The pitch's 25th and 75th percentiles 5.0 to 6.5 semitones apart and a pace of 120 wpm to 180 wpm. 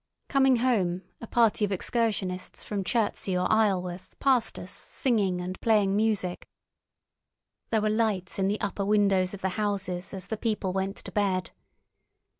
No: average, 3.0 semitones; average, 155 wpm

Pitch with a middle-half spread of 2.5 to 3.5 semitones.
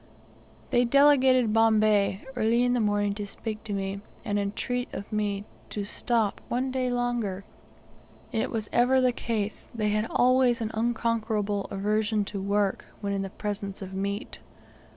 Yes: average, 3.0 semitones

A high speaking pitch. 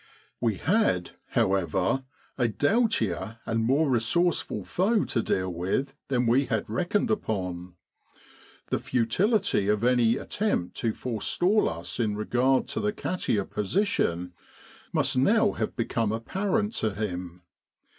No: low, 115 Hz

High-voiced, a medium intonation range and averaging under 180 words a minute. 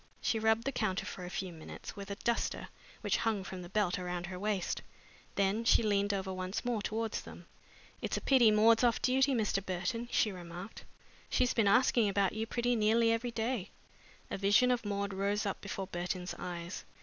No: high, 205 Hz; average, 3.3 semitones; average, 195 wpm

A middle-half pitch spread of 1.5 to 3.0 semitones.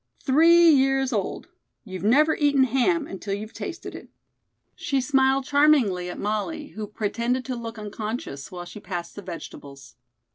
No: wide, 5.5 semitones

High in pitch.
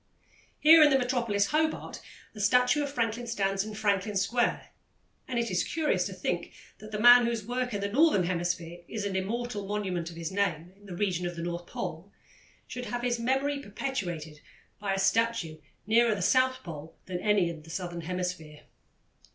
Yes: high, 205 Hz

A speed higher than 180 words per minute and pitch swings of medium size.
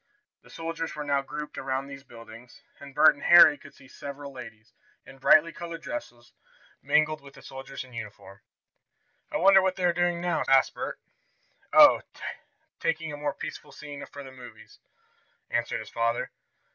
No: average, 170 wpm; average, 4.4 semitones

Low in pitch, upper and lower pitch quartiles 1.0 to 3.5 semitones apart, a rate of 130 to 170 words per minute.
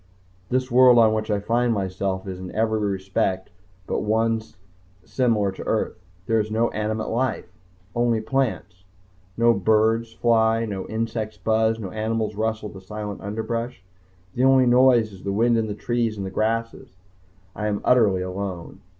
Yes: low, 110 Hz; narrow, 2.4 semitones; average, 160 wpm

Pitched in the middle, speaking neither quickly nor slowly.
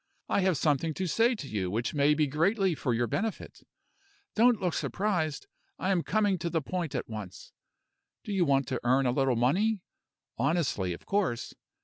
Yes: medium, 155 Hz; average, 185 wpm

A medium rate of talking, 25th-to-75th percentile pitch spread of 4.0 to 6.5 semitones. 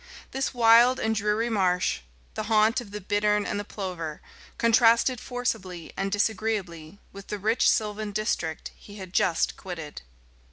No: average, 150 wpm; average, 3.1 semitones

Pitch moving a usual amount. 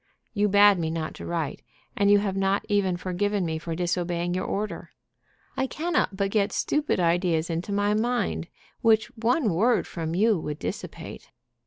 Yes: average, 3.6 semitones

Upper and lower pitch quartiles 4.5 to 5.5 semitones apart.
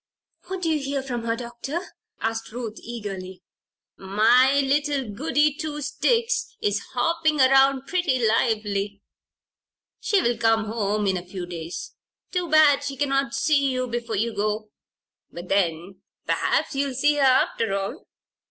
Yes: average, 5.2 semitones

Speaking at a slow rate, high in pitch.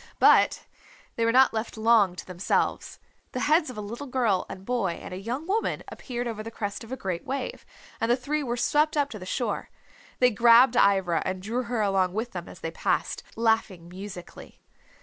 No: fast, 205 wpm; high, 230 Hz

